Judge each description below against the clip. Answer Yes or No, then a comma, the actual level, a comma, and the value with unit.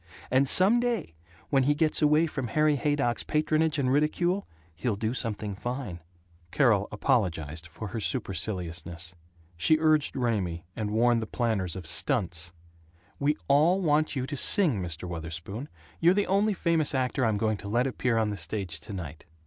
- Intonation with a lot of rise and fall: Yes, wide, 8.1 semitones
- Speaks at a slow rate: No, average, 165 wpm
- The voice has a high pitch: No, low, 120 Hz